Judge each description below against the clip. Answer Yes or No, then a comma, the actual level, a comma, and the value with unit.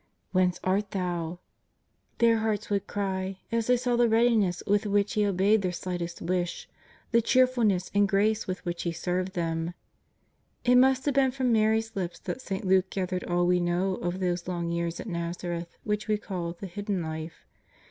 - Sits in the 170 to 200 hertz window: Yes, high, 190 Hz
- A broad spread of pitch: No, average, 3.7 semitones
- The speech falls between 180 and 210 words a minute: Yes, average, 190 wpm